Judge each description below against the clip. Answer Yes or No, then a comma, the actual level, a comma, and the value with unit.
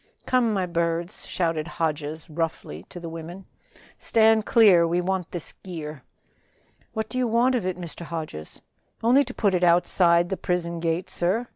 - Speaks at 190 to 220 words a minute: No, average, 165 wpm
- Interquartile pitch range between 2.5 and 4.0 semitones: Yes, average, 3.4 semitones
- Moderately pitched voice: Yes, medium, 175 Hz